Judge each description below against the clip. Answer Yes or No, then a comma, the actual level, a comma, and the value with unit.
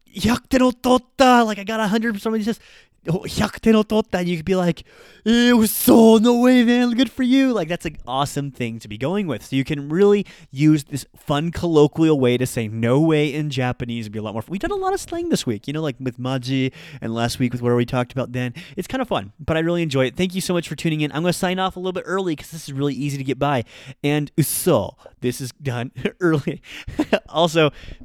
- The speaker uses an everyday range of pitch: No, wide, 7.9 semitones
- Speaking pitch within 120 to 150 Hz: No, medium, 160 Hz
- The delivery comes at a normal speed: No, fast, 240 wpm